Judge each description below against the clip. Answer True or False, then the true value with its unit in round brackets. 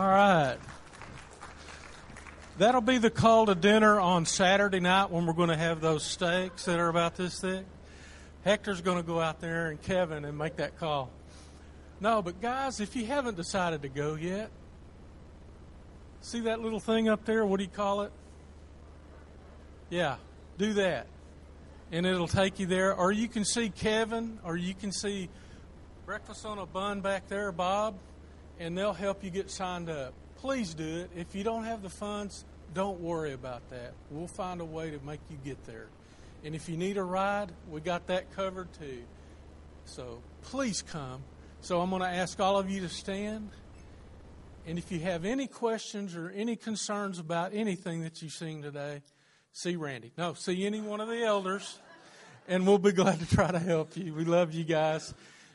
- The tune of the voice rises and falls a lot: True (5.7 semitones)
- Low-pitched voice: False (175 Hz)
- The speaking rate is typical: True (185 wpm)